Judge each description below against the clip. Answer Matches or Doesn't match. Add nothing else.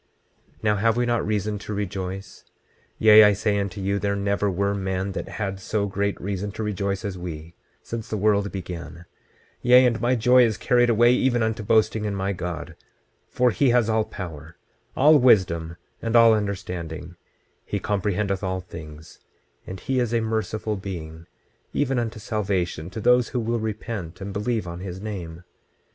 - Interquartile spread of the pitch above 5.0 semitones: Doesn't match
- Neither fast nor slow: Matches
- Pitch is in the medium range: Doesn't match